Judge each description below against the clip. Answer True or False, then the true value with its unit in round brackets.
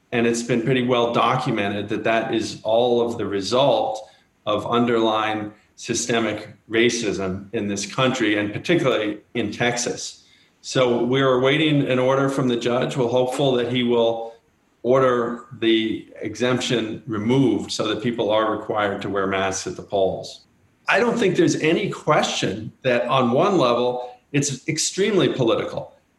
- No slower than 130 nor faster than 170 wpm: True (150 wpm)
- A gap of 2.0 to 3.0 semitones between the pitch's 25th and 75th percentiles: True (2.7 semitones)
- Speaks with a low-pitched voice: True (120 Hz)